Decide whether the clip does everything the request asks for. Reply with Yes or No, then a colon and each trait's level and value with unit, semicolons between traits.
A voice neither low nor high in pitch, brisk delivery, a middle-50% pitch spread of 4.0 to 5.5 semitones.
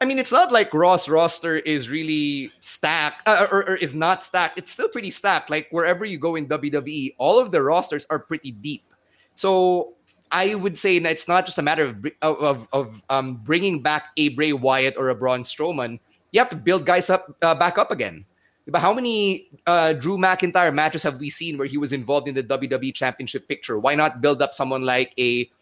Yes: medium, 155 Hz; fast, 215 wpm; average, 4.6 semitones